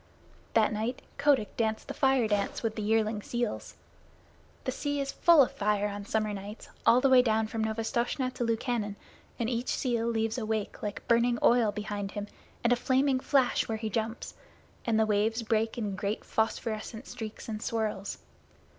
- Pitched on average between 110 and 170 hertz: No, high, 225 Hz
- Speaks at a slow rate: No, average, 180 wpm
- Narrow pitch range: Yes, narrow, 2.2 semitones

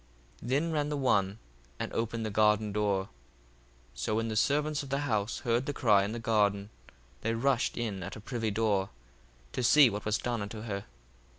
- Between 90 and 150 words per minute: No, average, 200 wpm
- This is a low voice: Yes, low, 110 Hz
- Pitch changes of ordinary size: Yes, average, 3.3 semitones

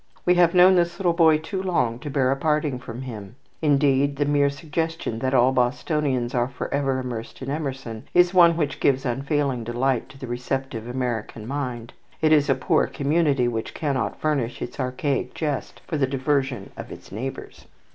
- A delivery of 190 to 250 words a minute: No, average, 180 wpm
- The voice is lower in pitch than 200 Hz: Yes, low, 135 Hz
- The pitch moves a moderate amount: Yes, average, 3.3 semitones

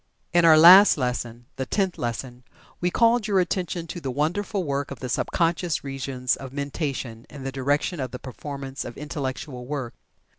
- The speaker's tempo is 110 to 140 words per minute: No, average, 180 wpm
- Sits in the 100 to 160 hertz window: Yes, medium, 140 Hz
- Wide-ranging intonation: No, average, 4.8 semitones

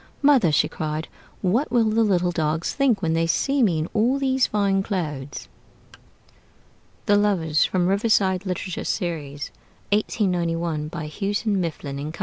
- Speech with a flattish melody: No, average, 4.7 semitones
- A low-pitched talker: No, medium, 185 Hz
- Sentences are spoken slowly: No, average, 145 wpm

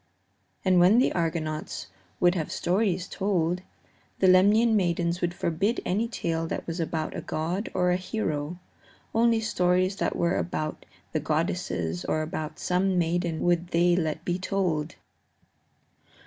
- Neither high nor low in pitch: Yes, medium, 175 Hz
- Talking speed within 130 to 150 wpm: Yes, average, 145 wpm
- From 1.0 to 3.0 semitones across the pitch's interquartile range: Yes, narrow, 2.5 semitones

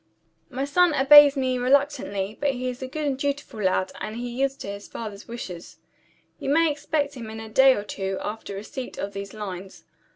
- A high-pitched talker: Yes, very high, 250 Hz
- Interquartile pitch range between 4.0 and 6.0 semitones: Yes, wide, 5.5 semitones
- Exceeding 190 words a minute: Yes, average, 200 wpm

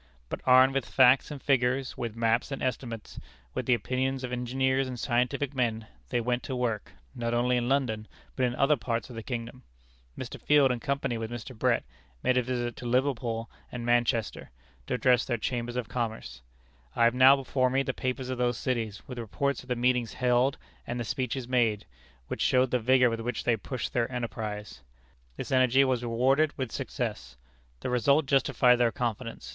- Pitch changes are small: Yes, narrow, 1.8 semitones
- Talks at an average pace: Yes, average, 190 wpm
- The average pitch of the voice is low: Yes, low, 125 Hz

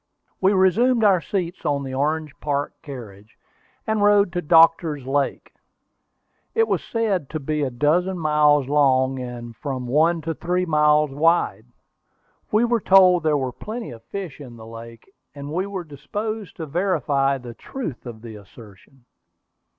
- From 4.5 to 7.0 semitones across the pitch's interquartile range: Yes, wide, 5.6 semitones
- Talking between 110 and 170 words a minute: Yes, average, 160 wpm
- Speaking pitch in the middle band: Yes, medium, 150 Hz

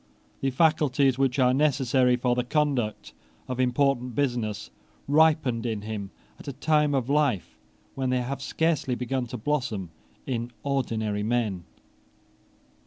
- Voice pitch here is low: Yes, low, 125 Hz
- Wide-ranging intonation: No, average, 3.0 semitones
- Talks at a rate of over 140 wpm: No, slow, 135 wpm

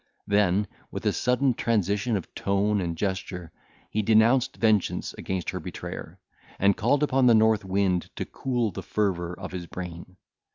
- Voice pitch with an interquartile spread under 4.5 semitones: Yes, average, 3.3 semitones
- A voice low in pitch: Yes, low, 100 Hz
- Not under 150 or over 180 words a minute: Yes, average, 160 wpm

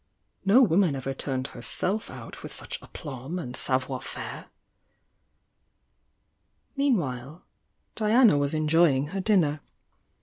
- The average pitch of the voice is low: No, medium, 155 Hz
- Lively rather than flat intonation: Yes, wide, 6.7 semitones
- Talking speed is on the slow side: Yes, slow, 105 wpm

